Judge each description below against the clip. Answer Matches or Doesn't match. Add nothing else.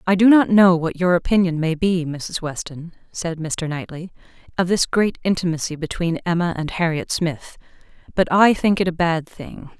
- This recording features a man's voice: Doesn't match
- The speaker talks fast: Doesn't match